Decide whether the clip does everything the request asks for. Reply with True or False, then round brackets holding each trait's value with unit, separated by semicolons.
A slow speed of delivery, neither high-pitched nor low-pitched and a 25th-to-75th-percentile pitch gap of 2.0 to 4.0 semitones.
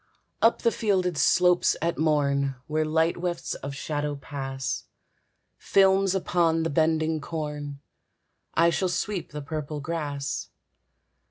True (120 wpm; 160 Hz; 3.2 semitones)